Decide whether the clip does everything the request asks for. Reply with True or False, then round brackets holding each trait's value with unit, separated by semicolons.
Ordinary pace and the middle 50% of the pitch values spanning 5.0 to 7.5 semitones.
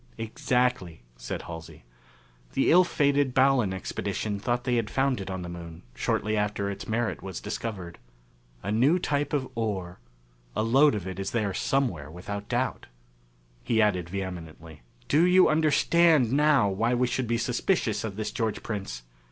True (160 wpm; 5.6 semitones)